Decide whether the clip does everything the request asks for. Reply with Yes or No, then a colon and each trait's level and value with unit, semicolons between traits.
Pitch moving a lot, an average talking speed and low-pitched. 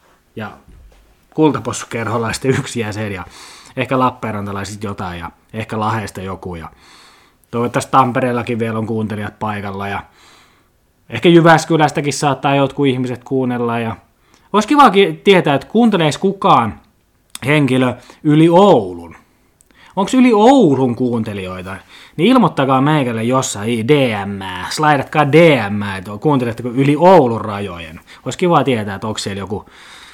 Yes: wide, 6.1 semitones; average, 115 wpm; low, 125 Hz